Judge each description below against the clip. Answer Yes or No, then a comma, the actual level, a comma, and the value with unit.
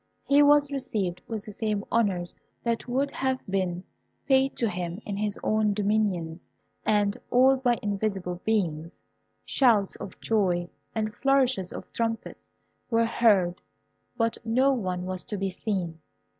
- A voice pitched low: No, high, 210 Hz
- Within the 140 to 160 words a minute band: Yes, average, 145 wpm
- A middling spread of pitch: Yes, average, 4.2 semitones